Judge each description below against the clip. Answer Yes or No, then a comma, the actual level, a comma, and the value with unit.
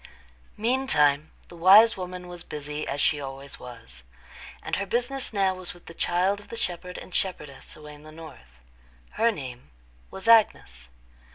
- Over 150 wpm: Yes, average, 165 wpm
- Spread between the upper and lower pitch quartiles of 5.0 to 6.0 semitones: Yes, wide, 5.5 semitones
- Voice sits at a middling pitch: Yes, medium, 175 Hz